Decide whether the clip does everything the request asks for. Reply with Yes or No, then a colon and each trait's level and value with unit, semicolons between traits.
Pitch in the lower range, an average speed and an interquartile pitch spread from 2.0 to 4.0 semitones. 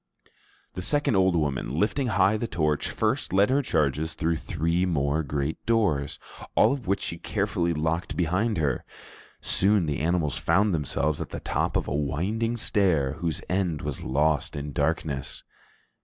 No: very low, 85 Hz; average, 160 wpm; average, 5.0 semitones